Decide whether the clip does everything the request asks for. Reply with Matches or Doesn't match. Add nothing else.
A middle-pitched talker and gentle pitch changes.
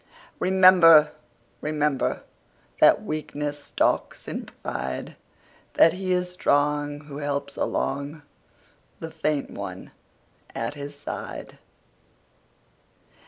Matches